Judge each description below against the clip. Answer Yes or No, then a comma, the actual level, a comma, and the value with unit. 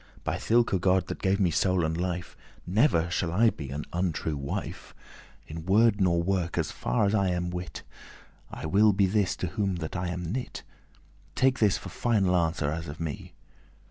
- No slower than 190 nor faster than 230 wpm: Yes, average, 195 wpm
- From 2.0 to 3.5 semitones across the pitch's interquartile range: Yes, average, 3.2 semitones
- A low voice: Yes, very low, 90 Hz